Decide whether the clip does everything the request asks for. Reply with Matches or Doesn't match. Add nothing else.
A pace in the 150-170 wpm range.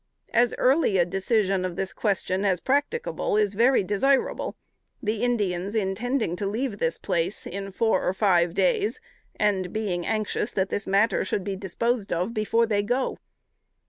Matches